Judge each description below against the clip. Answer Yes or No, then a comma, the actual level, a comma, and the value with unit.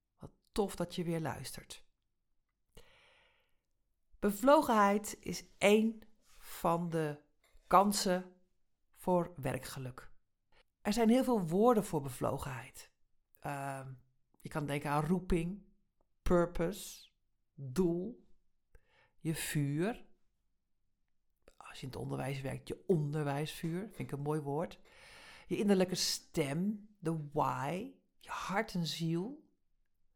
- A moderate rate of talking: No, slow, 105 wpm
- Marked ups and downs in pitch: Yes, wide, 5.7 semitones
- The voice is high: No, medium, 180 Hz